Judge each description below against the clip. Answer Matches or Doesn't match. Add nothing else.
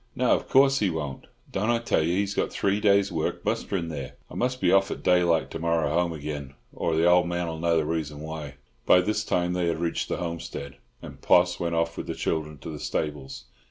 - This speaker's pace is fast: Matches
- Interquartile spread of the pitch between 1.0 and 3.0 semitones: Matches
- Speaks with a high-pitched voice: Doesn't match